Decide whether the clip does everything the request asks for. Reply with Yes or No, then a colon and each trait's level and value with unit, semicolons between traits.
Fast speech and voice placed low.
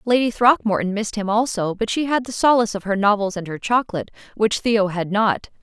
No: fast, 215 wpm; high, 215 Hz